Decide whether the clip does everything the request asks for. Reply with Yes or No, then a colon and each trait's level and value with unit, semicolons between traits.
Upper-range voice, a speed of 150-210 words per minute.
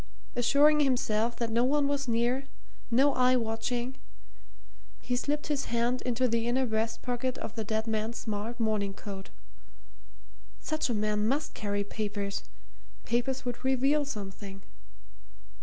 No: high, 235 Hz; average, 140 wpm